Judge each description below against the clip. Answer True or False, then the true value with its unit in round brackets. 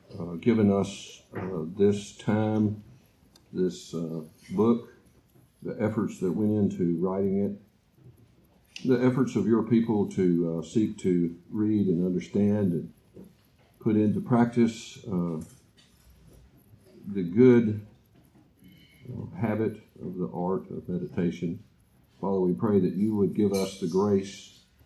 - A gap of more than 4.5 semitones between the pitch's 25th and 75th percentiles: False (3.3 semitones)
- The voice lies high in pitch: False (105 Hz)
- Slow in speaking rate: True (125 wpm)